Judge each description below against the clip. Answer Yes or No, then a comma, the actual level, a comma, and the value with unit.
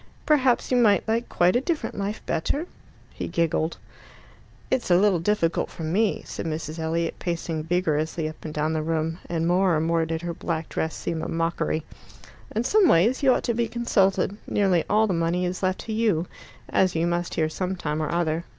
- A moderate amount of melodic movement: Yes, average, 4.3 semitones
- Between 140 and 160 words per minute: No, average, 200 wpm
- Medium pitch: Yes, medium, 175 Hz